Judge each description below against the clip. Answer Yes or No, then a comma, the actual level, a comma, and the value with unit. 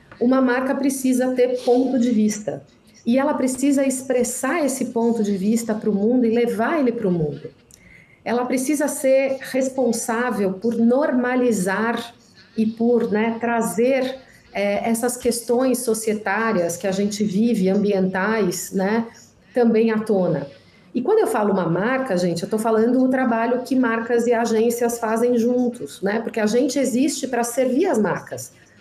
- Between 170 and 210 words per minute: No, average, 155 wpm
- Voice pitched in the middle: No, high, 235 Hz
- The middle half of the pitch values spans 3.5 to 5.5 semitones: No, average, 3.1 semitones